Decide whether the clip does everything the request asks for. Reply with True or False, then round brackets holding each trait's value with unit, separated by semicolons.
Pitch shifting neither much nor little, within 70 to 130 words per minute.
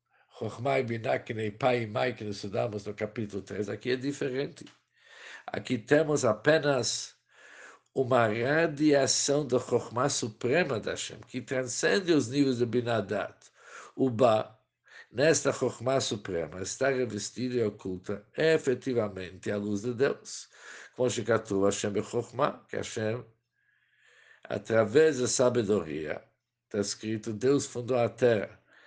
True (3.5 semitones; 125 wpm)